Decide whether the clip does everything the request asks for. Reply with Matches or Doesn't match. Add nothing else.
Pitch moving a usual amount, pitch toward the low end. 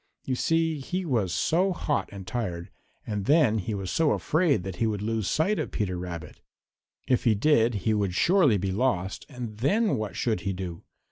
Doesn't match